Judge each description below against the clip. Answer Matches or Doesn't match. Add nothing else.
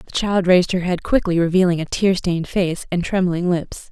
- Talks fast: Matches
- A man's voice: Doesn't match